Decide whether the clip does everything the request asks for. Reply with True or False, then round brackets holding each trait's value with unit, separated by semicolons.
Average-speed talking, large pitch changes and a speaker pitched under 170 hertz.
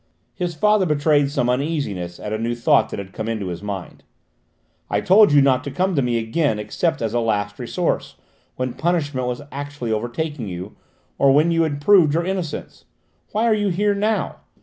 True (195 wpm; 6.6 semitones; 140 Hz)